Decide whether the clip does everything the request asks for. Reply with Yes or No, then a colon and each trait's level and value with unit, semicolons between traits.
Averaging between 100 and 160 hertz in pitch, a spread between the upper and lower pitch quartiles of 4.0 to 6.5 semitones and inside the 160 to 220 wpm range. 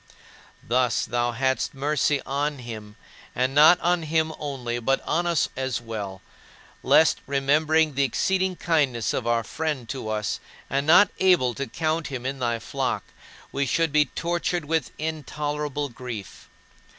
No: medium, 140 Hz; average, 4.5 semitones; average, 150 wpm